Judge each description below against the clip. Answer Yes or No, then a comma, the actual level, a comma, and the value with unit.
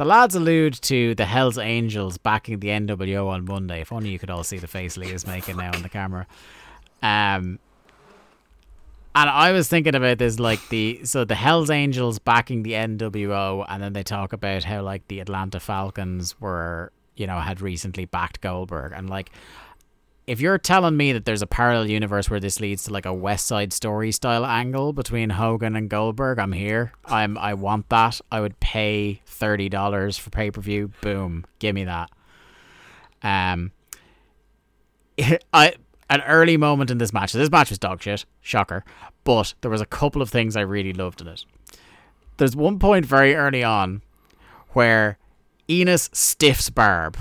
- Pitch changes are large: No, average, 3.7 semitones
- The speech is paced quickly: No, average, 180 wpm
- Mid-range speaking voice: No, low, 105 Hz